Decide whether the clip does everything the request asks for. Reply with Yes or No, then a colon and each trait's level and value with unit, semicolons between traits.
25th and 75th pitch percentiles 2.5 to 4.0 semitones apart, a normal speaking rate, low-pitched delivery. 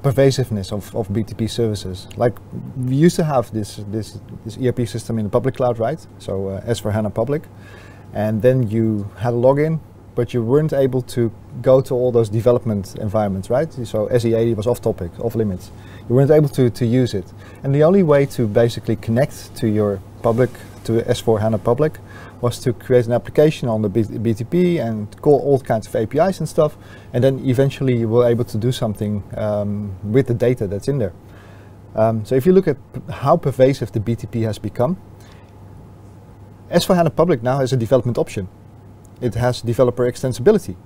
Yes: average, 3.7 semitones; average, 185 wpm; low, 115 Hz